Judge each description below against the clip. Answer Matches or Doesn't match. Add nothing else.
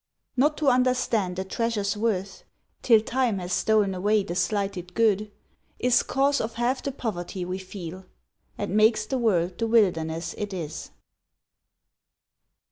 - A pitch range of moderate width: Matches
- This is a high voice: Matches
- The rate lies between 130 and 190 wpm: Matches